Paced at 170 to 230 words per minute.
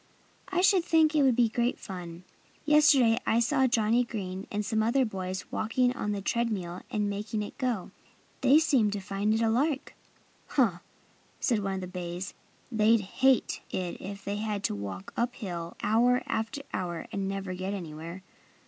Yes: average, 180 wpm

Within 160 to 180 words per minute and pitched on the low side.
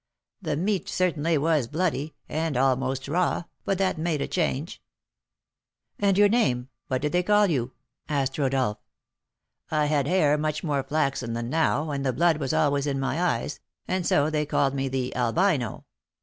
No: average, 170 wpm; medium, 150 Hz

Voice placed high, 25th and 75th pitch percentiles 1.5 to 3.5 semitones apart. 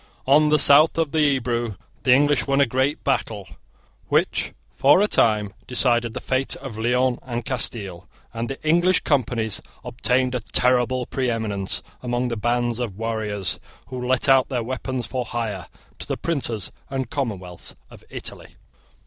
No: low, 125 Hz; average, 2.9 semitones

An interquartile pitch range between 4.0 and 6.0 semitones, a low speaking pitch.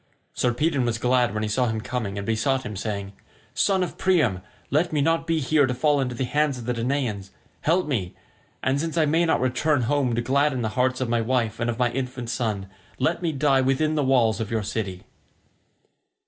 Yes: average, 4.3 semitones; low, 125 Hz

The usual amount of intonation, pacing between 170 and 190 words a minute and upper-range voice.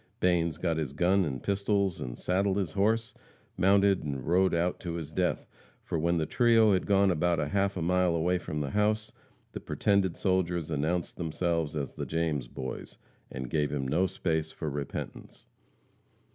No: average, 3.8 semitones; average, 175 wpm; very low, 85 Hz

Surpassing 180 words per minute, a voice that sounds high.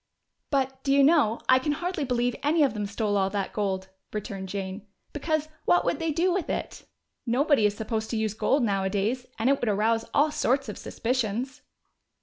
Yes: average, 190 wpm; high, 235 Hz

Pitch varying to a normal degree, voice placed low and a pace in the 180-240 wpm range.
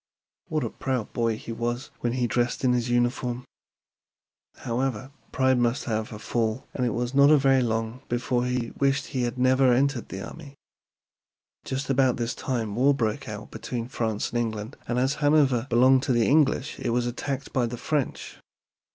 No: narrow, 2.2 semitones; low, 125 Hz; average, 185 wpm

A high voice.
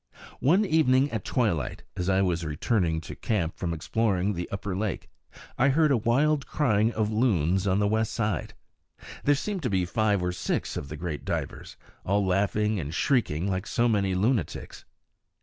No: low, 105 Hz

